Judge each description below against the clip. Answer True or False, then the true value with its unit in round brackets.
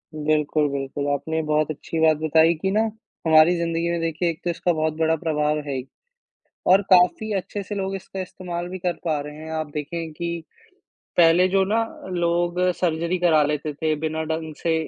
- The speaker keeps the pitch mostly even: True (2.3 semitones)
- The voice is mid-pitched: True (160 Hz)